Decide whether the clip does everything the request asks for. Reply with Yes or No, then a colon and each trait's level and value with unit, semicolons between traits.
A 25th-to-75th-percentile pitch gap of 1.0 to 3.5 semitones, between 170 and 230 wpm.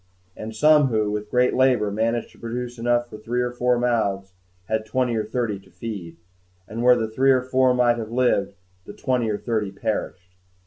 Yes: narrow, 2.6 semitones; average, 195 wpm